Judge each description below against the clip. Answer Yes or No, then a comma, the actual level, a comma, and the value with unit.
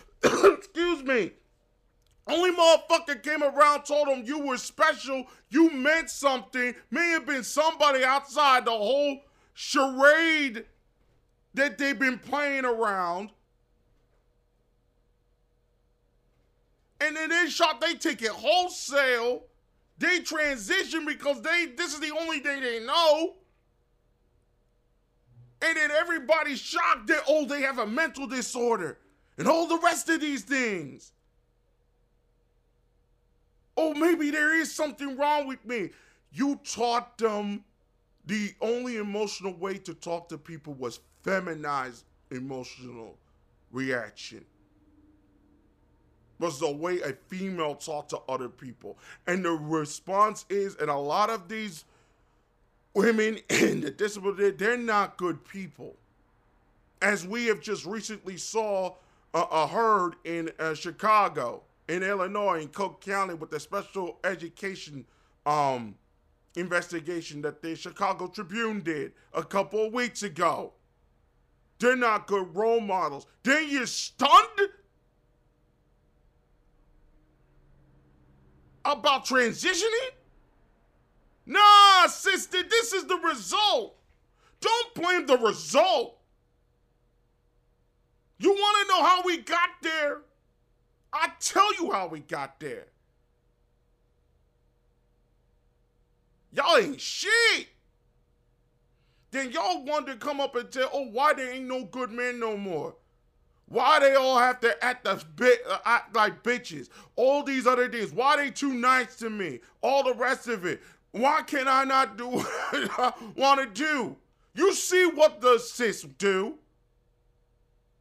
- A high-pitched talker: Yes, high, 245 Hz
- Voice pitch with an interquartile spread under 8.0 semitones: No, wide, 8.5 semitones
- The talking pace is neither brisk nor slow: No, slow, 125 wpm